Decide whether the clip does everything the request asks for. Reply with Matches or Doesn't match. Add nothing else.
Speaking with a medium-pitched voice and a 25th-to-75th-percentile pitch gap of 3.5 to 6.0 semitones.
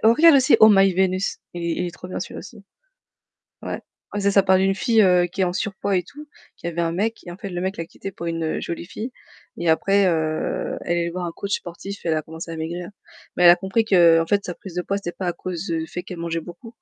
Doesn't match